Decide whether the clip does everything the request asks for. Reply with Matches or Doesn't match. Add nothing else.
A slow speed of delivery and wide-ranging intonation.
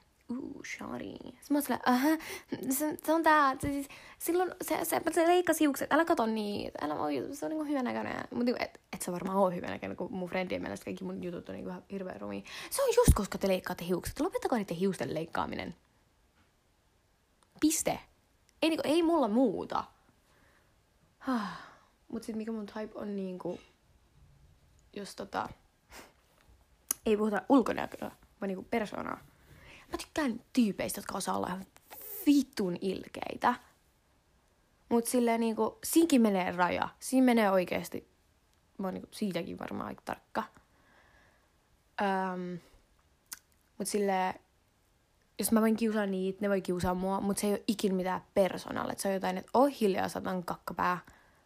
Doesn't match